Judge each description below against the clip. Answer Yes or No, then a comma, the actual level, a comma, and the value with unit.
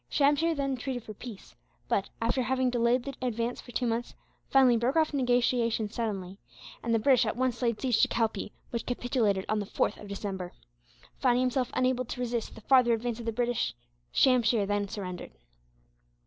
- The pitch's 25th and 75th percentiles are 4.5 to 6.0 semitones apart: No, average, 2.7 semitones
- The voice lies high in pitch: Yes, high, 240 Hz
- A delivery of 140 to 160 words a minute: No, average, 180 wpm